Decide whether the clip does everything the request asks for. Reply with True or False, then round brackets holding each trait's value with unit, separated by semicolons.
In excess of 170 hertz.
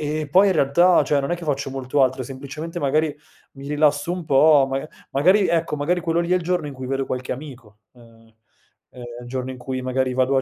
False (140 Hz)